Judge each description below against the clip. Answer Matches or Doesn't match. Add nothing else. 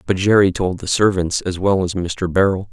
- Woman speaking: Doesn't match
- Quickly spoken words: Matches